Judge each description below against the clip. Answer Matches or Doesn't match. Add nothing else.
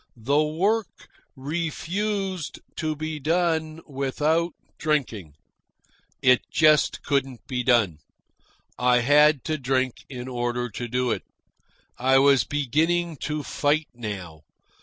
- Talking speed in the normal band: Doesn't match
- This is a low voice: Doesn't match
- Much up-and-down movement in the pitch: Doesn't match